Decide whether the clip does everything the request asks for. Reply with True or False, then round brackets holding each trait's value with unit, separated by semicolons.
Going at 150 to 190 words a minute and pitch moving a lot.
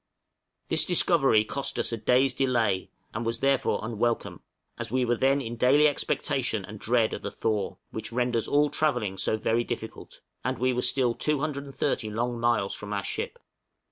False (170 wpm; 3.4 semitones)